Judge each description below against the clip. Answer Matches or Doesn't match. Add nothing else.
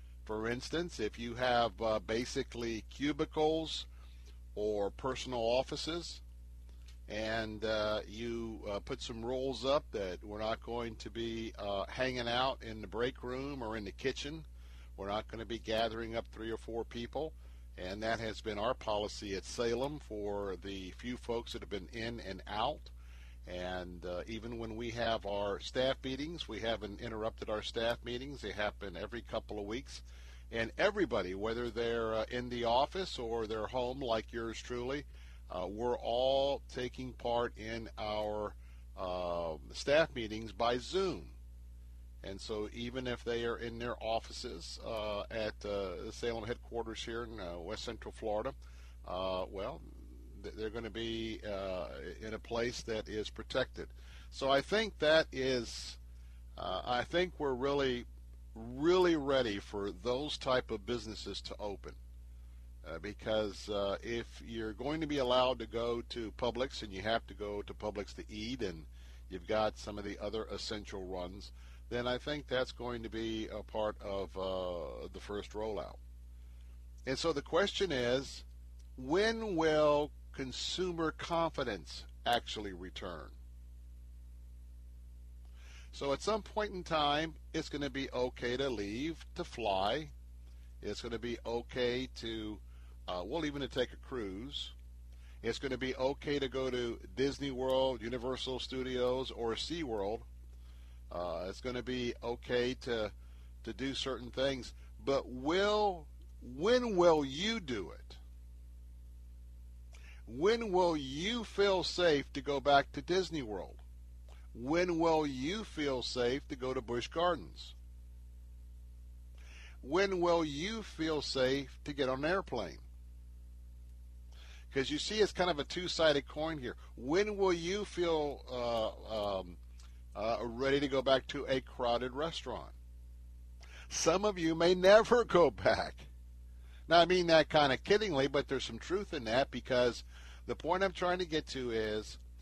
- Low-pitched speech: Matches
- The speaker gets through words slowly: Doesn't match